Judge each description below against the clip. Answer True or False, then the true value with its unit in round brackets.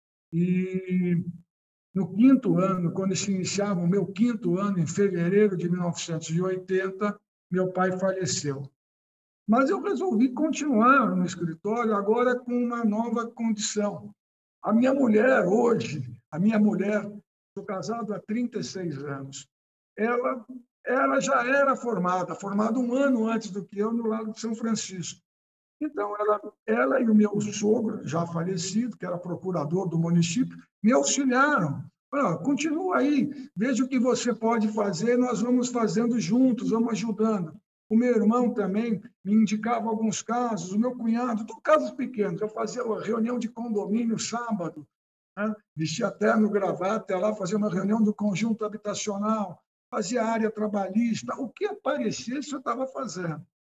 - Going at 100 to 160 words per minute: True (150 wpm)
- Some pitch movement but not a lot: True (4.0 semitones)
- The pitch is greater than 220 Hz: False (215 Hz)